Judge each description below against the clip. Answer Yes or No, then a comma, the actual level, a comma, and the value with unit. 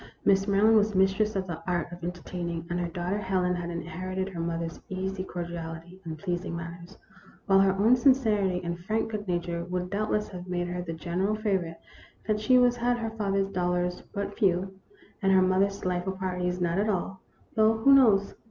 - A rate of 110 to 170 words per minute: No, average, 200 wpm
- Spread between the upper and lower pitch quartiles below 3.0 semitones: Yes, narrow, 2.5 semitones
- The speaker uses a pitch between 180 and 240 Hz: Yes, medium, 185 Hz